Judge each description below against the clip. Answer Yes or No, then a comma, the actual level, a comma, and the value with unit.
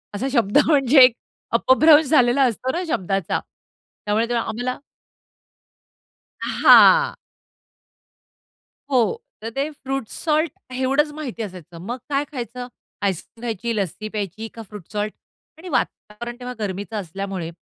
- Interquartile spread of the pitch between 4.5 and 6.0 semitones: Yes, average, 4.8 semitones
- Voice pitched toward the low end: No, high, 240 Hz